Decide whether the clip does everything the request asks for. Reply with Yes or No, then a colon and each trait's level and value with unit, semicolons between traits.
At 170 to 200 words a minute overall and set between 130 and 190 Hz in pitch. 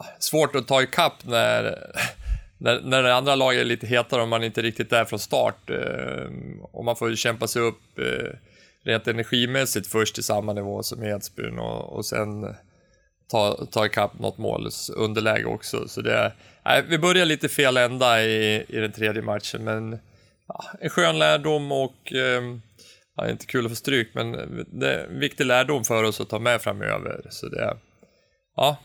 No: average, 185 wpm; low, 115 Hz